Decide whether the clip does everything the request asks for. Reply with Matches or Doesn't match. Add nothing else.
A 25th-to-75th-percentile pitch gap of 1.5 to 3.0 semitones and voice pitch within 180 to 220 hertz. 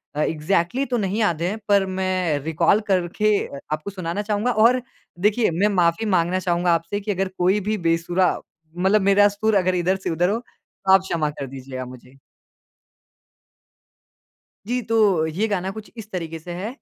Doesn't match